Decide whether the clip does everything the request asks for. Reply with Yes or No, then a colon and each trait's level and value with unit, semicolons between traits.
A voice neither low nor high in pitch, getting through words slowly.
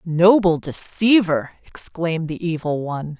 Yes: medium, 170 Hz; slow, 115 wpm